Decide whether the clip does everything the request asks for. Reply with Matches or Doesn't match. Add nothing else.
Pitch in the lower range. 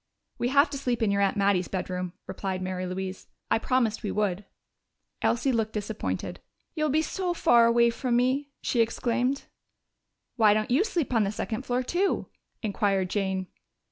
Doesn't match